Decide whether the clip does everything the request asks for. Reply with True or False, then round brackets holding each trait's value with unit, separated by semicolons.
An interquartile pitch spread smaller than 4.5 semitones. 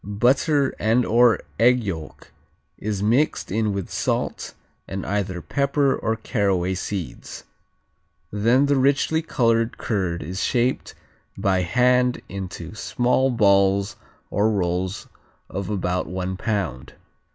False (4.8 semitones)